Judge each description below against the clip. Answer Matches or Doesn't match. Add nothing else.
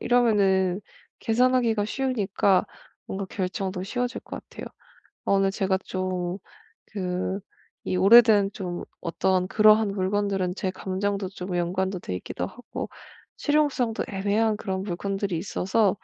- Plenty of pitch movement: Doesn't match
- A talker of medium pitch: Doesn't match